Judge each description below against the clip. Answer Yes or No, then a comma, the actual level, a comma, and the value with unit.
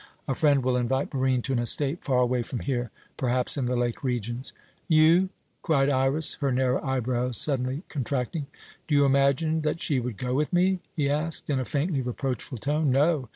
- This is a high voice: No, low, 135 Hz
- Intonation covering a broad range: No, average, 2.9 semitones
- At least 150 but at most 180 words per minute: No, average, 190 wpm